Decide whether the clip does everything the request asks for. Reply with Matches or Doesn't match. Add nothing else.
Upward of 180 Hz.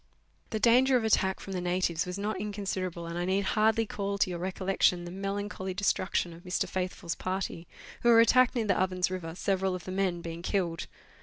Matches